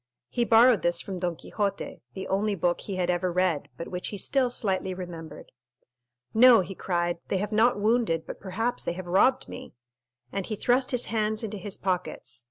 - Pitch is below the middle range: No, high, 195 Hz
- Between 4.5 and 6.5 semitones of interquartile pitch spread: No, average, 3.8 semitones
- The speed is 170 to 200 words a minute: Yes, average, 190 wpm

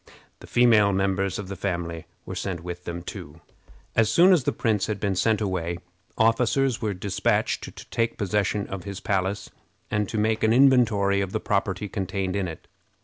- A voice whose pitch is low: Yes, low, 100 Hz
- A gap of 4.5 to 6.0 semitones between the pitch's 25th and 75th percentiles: No, average, 2.8 semitones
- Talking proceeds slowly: No, average, 185 wpm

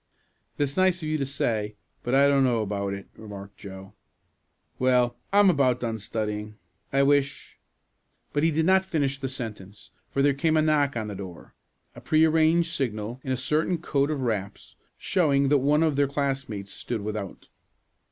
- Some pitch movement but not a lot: No, wide, 5.7 semitones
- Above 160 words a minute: Yes, average, 180 wpm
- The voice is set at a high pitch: No, low, 135 Hz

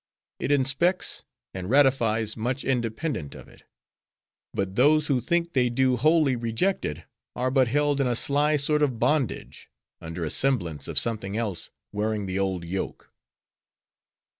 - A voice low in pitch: Yes, low, 125 Hz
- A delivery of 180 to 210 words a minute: No, average, 150 wpm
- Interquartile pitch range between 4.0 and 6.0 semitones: Yes, wide, 5.6 semitones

